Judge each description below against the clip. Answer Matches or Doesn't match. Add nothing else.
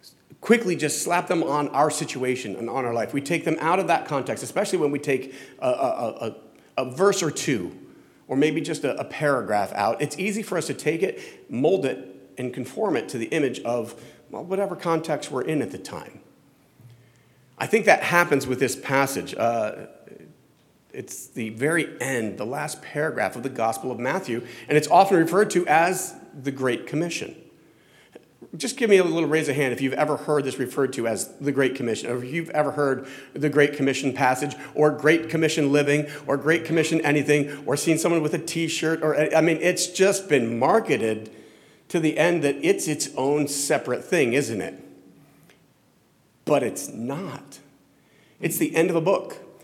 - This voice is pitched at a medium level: Matches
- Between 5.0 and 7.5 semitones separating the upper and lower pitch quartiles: Doesn't match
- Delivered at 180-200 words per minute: Matches